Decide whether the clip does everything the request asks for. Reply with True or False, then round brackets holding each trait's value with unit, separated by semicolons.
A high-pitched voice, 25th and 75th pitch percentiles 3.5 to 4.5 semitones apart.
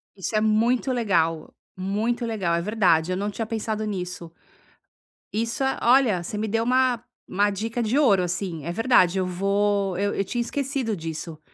True (205 Hz; 4.0 semitones)